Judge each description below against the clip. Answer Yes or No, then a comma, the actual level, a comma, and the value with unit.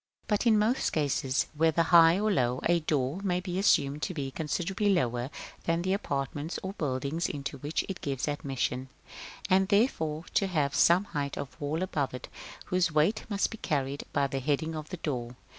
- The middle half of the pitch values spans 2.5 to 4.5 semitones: No, average, 4.9 semitones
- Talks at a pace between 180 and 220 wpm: Yes, average, 185 wpm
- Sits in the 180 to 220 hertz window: No, medium, 155 Hz